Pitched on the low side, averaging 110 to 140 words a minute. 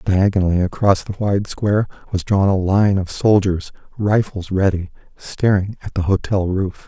No: very low, 95 Hz; average, 155 wpm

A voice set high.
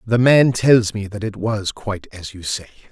No: low, 105 Hz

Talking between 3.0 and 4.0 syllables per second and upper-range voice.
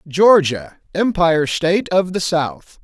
No: 3.9 syllables/s; medium, 175 Hz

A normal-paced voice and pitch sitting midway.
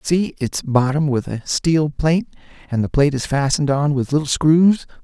Yes: average, 190 wpm; medium, 145 Hz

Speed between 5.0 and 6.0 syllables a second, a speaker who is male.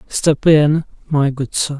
No: 3.5 syllables/s; male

